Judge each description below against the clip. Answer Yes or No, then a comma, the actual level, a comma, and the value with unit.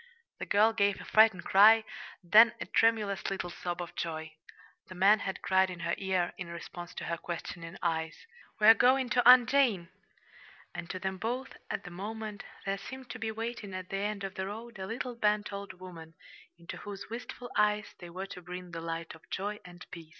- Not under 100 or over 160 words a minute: No, average, 200 wpm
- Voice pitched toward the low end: No, high, 195 Hz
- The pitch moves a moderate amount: Yes, average, 3.9 semitones